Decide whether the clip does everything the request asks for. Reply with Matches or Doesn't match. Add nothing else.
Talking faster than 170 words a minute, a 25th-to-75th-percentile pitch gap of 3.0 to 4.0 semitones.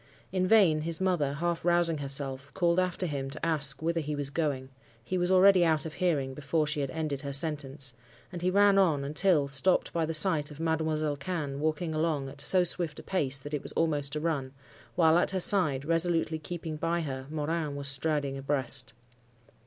Matches